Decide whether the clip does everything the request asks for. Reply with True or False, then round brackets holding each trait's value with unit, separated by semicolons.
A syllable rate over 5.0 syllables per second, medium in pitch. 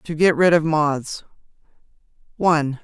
False (4.2 syllables/s; 155 Hz)